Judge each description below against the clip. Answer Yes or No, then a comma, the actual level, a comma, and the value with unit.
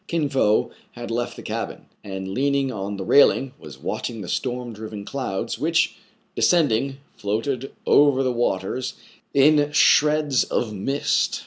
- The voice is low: Yes, low, 125 Hz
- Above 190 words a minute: No, average, 140 wpm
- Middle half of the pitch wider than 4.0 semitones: Yes, average, 4.9 semitones